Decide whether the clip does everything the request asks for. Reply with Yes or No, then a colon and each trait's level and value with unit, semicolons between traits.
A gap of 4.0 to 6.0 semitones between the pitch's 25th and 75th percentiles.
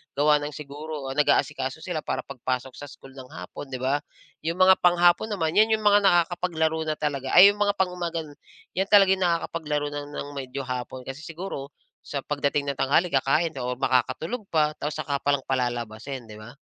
Yes: average, 4.4 semitones